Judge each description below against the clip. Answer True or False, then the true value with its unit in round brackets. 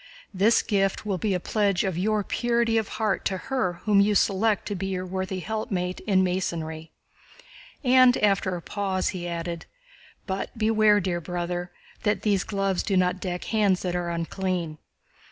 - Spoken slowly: False (170 wpm)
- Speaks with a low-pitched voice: False (190 Hz)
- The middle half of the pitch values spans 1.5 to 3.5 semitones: True (2.8 semitones)